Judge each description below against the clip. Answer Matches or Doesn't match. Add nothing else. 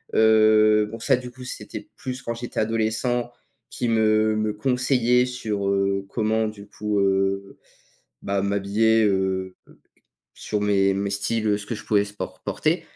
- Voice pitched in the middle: Doesn't match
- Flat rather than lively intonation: Matches